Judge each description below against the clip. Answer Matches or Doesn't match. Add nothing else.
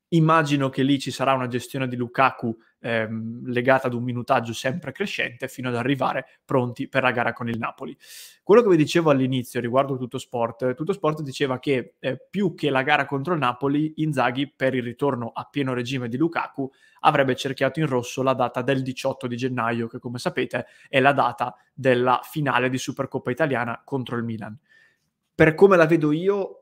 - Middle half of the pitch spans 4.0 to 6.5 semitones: Doesn't match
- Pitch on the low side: Matches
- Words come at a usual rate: Doesn't match